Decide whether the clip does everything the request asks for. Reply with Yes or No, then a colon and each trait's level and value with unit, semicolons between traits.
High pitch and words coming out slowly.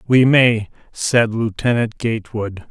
No: low, 115 Hz; slow, 110 wpm